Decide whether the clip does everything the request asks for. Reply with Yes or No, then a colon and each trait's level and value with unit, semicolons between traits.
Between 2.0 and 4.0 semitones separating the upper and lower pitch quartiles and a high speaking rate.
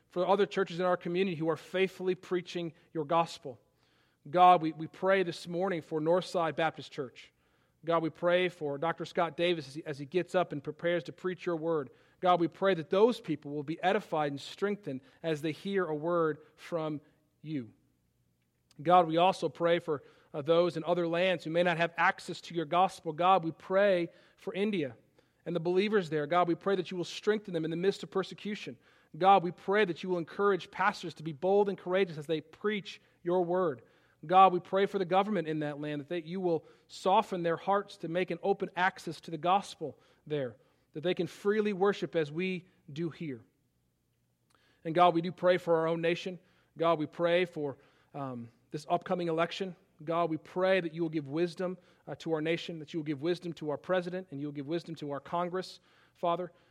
Yes: narrow, 2.6 semitones; fast, 210 wpm